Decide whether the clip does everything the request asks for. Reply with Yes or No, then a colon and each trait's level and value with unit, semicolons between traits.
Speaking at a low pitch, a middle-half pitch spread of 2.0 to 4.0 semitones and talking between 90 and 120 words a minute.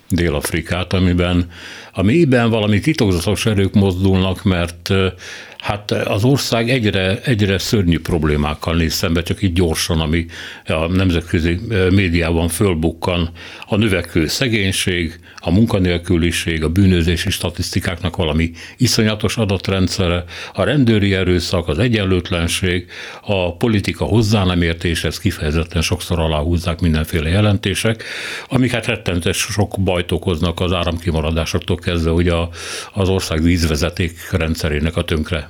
Yes: very low, 90 Hz; average, 2.9 semitones; average, 115 wpm